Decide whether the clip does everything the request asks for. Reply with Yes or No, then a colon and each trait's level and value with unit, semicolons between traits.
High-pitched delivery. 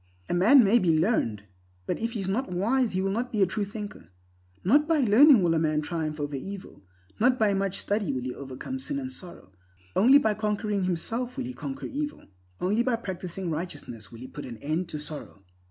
Yes: high, 195 Hz